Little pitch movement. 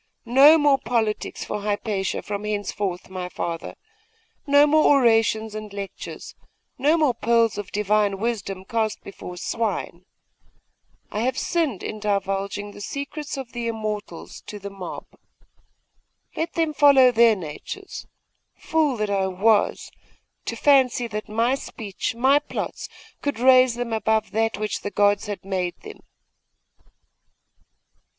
No: average, 4.1 semitones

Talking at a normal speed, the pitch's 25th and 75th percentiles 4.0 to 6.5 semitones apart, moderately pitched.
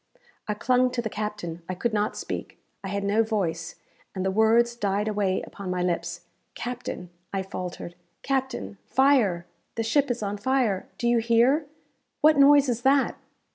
No: average, 170 wpm; average, 4.6 semitones; high, 215 Hz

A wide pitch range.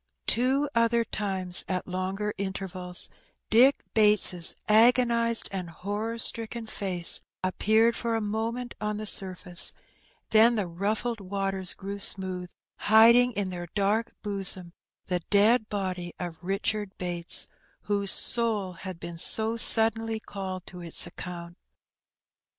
No: average, 3.4 semitones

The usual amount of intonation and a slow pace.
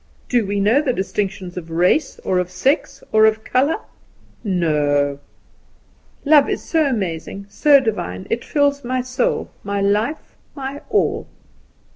No: wide, 7.1 semitones; slow, 130 wpm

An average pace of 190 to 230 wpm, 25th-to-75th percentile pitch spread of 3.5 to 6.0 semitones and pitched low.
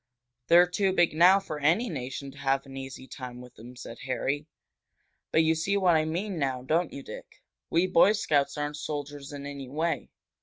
No: average, 195 wpm; average, 4.1 semitones; medium, 145 Hz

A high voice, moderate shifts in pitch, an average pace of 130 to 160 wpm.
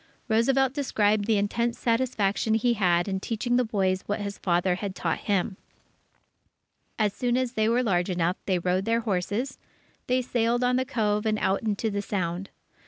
No: high, 210 Hz; average, 3.6 semitones; average, 175 wpm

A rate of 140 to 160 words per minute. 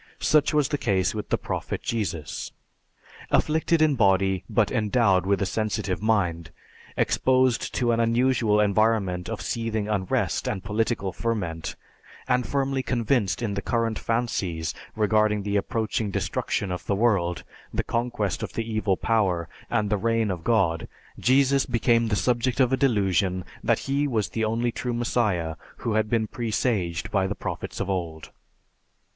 Yes: average, 155 wpm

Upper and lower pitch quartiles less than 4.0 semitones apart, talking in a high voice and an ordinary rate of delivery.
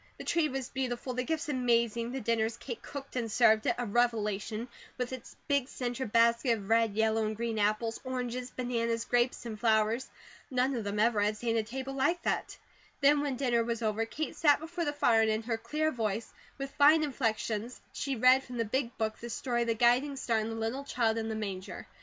No: average, 2.8 semitones; high, 235 Hz; fast, 220 wpm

